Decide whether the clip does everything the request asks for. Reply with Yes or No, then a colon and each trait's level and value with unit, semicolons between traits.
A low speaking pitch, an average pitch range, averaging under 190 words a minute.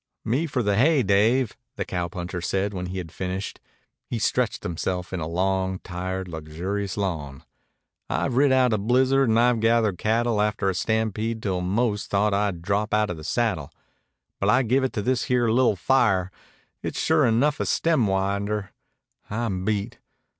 Yes: low, 105 Hz; average, 4.1 semitones; average, 170 wpm